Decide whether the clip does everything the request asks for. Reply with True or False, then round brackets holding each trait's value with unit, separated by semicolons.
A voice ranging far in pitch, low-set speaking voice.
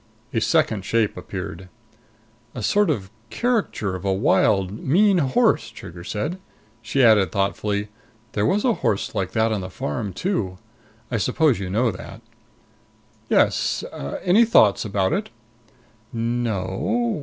True (8.0 semitones; 110 Hz)